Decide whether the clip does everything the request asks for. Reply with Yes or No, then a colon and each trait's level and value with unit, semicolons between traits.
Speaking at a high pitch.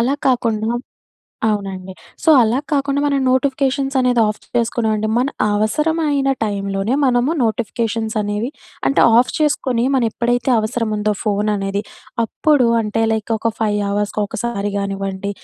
Yes: high, 225 Hz